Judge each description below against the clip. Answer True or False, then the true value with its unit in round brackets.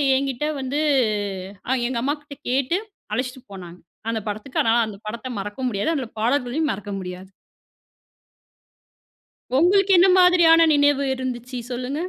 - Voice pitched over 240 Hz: True (260 Hz)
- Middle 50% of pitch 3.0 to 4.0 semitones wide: False (4.6 semitones)